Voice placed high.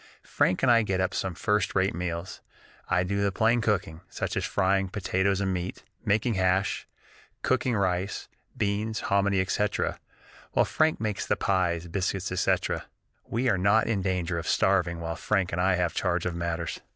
No: very low, 95 Hz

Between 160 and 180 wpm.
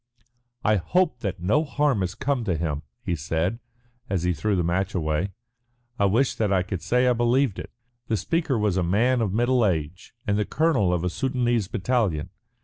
No: average, 195 wpm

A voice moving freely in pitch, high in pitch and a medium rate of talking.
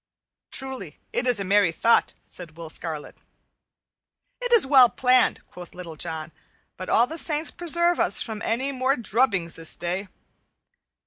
Yes: wide, 7.5 semitones; high, 220 Hz; average, 150 wpm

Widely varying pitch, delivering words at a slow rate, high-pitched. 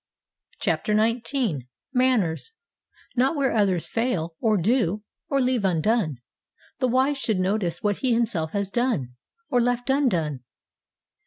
Yes: wide, 5.7 semitones; slow, 125 wpm; high, 225 Hz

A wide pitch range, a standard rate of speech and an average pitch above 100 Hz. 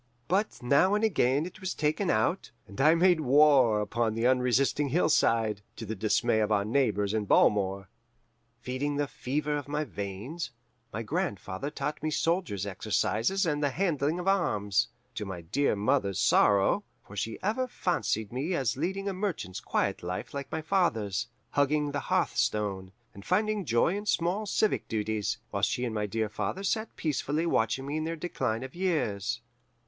Yes: wide, 7.6 semitones; average, 170 wpm; low, 135 Hz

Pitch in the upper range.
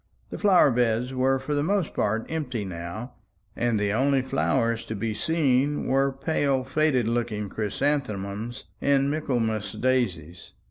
No: low, 125 Hz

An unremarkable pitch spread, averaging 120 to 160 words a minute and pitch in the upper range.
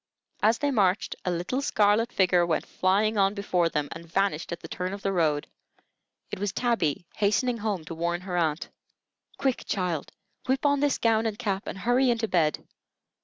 No: average, 4.5 semitones; average, 185 wpm; high, 195 Hz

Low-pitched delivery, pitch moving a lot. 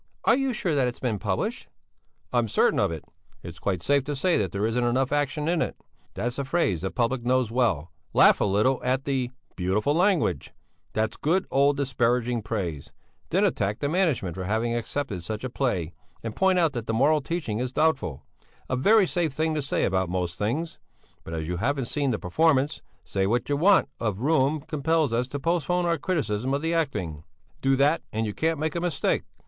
Yes: low, 130 Hz; wide, 6.5 semitones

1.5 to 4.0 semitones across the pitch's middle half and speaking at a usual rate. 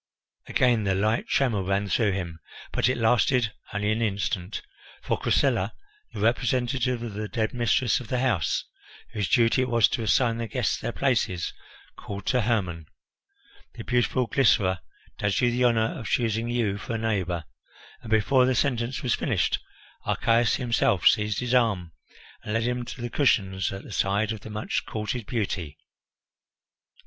Yes: average, 3.2 semitones; average, 165 wpm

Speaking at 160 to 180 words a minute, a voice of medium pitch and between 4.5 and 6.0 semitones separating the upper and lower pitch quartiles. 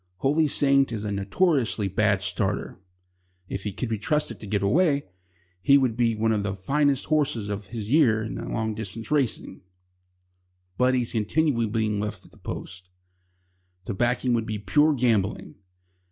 No: average, 170 wpm; low, 115 Hz; average, 4.9 semitones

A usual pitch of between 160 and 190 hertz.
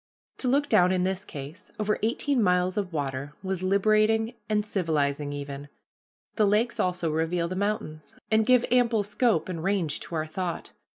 Yes: medium, 185 Hz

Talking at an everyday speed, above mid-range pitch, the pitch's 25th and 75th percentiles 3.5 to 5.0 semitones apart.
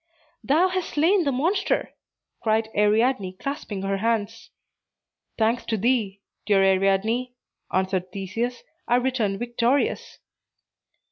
No: slow, 110 wpm; high, 225 Hz; average, 4.5 semitones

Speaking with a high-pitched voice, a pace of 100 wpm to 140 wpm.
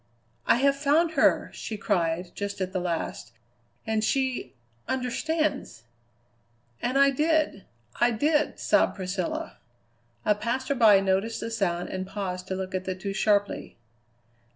Yes: high, 210 Hz; slow, 135 wpm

